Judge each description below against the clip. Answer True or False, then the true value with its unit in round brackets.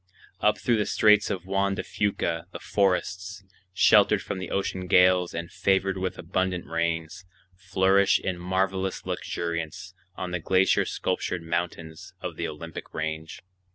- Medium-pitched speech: False (90 Hz)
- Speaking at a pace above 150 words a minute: False (145 wpm)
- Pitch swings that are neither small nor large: False (2.2 semitones)